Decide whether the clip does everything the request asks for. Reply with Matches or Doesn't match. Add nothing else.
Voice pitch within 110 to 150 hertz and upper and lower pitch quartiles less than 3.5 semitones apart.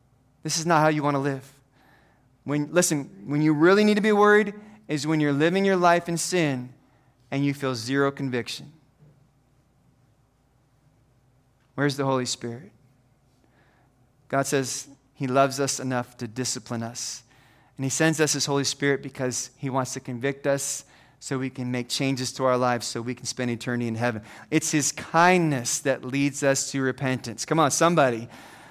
Matches